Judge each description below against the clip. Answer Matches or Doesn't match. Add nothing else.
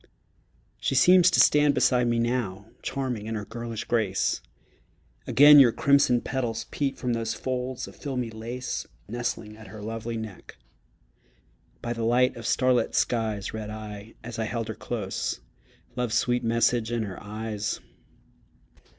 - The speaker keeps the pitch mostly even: Matches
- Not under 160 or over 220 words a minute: Doesn't match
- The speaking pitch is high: Doesn't match